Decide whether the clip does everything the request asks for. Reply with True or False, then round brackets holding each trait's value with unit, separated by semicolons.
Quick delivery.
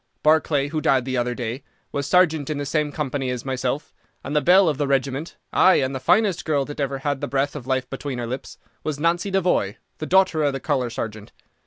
True (225 wpm)